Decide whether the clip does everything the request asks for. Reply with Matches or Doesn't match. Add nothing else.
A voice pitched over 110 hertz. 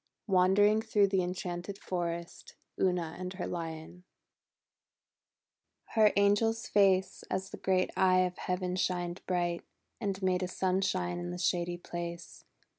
Matches